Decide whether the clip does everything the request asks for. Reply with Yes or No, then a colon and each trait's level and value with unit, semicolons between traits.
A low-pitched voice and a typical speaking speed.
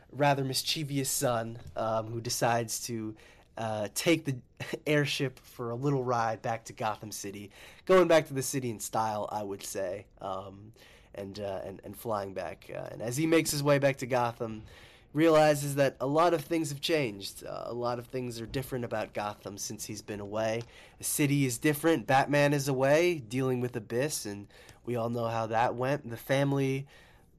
Yes: low, 120 Hz; average, 190 wpm